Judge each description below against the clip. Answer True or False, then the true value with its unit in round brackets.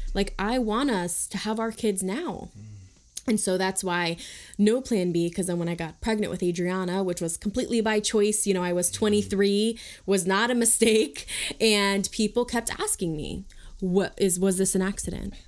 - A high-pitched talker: True (200 Hz)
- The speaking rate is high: False (190 wpm)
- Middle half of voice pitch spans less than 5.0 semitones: True (3.4 semitones)